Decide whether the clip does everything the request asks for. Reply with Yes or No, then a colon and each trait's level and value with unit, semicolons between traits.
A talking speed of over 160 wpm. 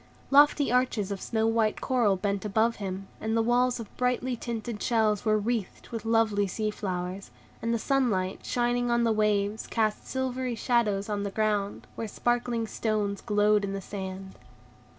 Yes: average, 170 wpm